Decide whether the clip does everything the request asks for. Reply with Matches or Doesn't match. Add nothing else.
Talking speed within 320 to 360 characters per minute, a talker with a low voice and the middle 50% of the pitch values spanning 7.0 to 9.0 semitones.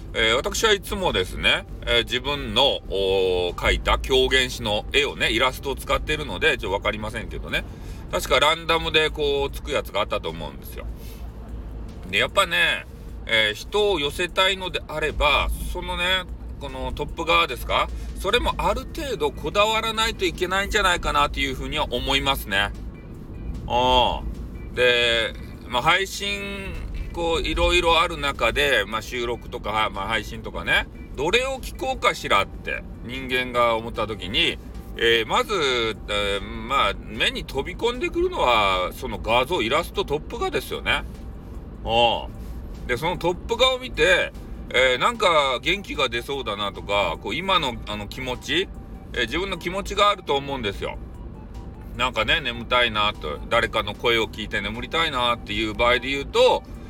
Matches